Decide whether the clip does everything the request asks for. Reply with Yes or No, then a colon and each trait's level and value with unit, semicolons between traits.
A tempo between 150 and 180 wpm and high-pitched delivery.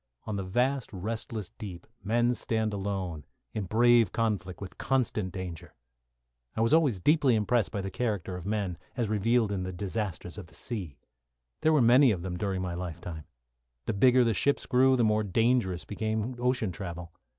No: average, 175 wpm; low, 105 Hz